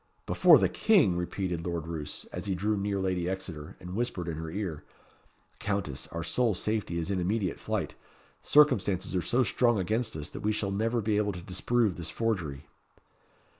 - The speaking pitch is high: No, very low, 95 Hz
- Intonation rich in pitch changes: No, average, 3.8 semitones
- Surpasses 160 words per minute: Yes, average, 180 wpm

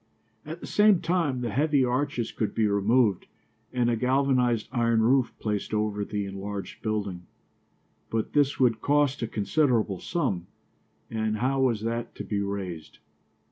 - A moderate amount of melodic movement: Yes, average, 4.2 semitones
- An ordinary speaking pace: Yes, average, 150 wpm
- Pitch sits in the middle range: No, low, 115 Hz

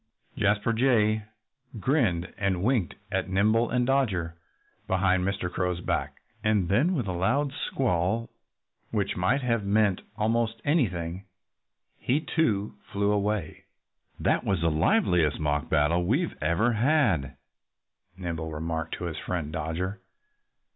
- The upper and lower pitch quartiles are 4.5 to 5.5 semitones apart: Yes, average, 5.1 semitones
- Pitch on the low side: Yes, low, 100 Hz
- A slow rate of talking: Yes, slow, 125 wpm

